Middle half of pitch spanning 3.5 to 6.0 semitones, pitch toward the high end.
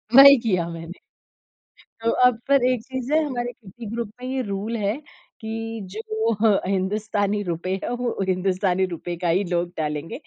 Yes: average, 4.3 semitones; high, 210 Hz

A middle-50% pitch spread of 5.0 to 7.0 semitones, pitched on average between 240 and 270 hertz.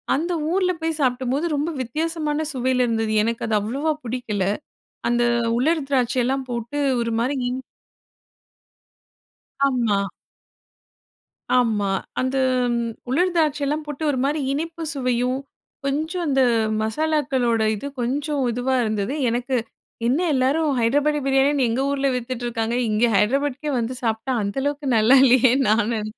No: average, 3.6 semitones; very high, 260 Hz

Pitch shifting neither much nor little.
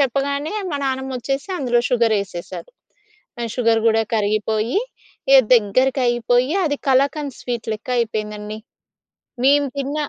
Yes: average, 3.8 semitones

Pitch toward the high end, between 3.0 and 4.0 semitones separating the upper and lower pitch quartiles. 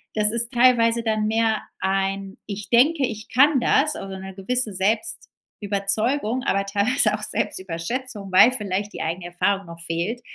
Yes: high, 210 Hz; average, 3.7 semitones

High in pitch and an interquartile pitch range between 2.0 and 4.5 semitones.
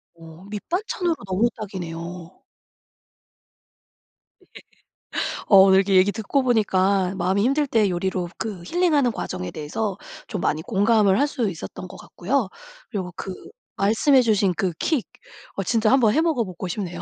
Yes: high, 200 Hz; average, 4.2 semitones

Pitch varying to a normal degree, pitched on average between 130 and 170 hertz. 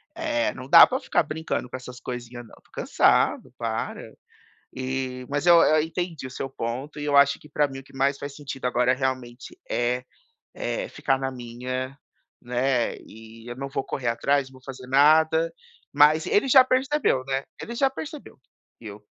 Yes: average, 3.7 semitones; low, 135 Hz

